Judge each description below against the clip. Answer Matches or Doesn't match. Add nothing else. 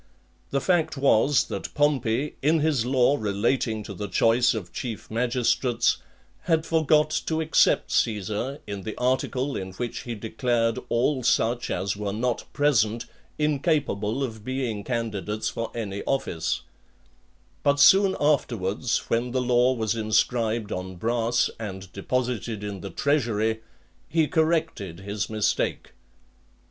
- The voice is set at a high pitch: Doesn't match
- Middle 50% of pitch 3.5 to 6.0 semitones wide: Matches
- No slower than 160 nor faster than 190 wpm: Doesn't match